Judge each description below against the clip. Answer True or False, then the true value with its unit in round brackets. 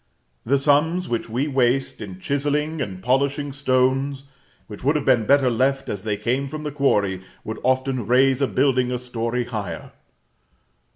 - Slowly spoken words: False (165 wpm)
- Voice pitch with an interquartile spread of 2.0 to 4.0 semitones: True (2.7 semitones)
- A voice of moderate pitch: False (130 Hz)